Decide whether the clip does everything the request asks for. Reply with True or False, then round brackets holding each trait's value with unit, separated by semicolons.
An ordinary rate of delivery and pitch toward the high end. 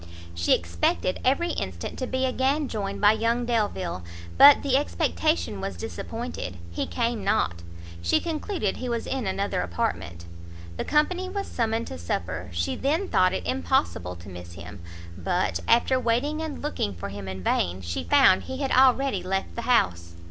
True (170 wpm; 205 Hz)